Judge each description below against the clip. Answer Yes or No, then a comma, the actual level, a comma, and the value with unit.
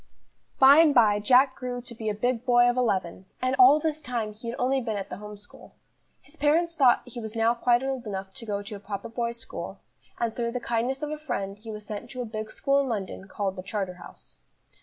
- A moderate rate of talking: No, fast, 240 wpm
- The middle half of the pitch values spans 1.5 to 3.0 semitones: No, average, 3.6 semitones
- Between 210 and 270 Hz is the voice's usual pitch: Yes, high, 235 Hz